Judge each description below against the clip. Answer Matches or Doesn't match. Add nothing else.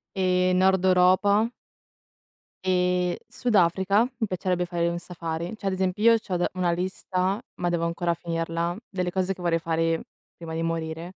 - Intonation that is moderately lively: Doesn't match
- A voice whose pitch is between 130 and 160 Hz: Doesn't match